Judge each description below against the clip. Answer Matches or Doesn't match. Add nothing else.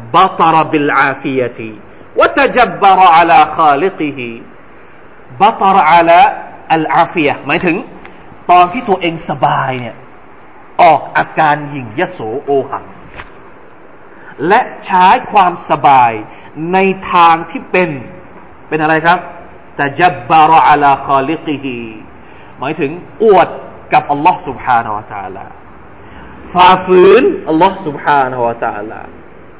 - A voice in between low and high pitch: Matches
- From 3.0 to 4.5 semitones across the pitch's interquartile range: Doesn't match